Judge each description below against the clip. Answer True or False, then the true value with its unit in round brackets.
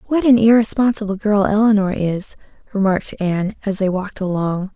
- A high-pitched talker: True (200 Hz)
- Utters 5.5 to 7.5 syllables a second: True (5.6 syllables/s)